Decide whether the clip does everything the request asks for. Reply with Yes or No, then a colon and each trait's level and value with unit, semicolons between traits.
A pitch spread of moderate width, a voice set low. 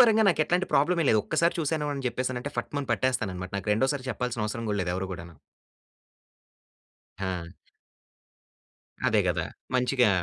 No: wide, 5.7 semitones; low, 125 Hz